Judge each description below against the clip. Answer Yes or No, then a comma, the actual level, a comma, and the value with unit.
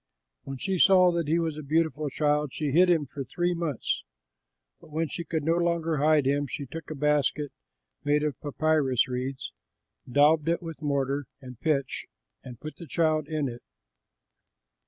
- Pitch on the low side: No, medium, 150 Hz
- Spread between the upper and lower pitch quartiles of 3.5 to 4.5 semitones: No, narrow, 2.6 semitones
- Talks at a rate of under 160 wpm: No, average, 175 wpm